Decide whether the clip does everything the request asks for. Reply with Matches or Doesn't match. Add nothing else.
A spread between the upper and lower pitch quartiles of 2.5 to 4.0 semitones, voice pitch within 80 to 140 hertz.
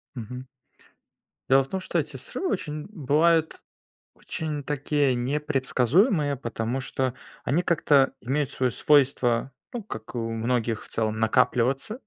Matches